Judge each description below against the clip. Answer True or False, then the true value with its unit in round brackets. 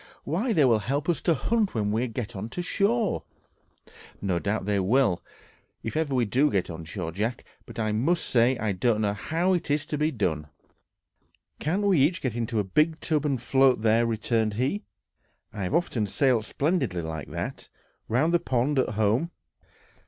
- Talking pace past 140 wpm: True (185 wpm)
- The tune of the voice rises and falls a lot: True (6.5 semitones)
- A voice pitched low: True (125 Hz)